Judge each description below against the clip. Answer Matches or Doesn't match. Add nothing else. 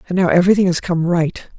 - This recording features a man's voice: Doesn't match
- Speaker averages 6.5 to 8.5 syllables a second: Matches